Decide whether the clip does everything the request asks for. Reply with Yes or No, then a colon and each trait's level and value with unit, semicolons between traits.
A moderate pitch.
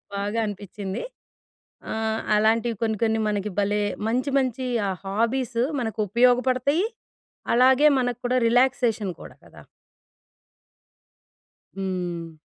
No: high, 225 Hz